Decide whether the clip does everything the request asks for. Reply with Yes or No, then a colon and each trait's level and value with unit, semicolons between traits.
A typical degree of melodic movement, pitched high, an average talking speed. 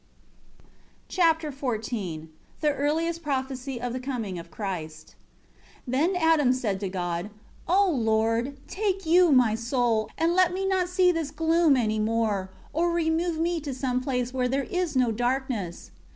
No: wide, 6.6 semitones; very high, 265 Hz; average, 155 wpm